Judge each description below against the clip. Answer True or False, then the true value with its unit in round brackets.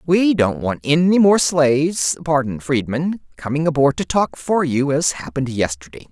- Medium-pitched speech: True (145 Hz)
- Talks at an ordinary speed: True (165 wpm)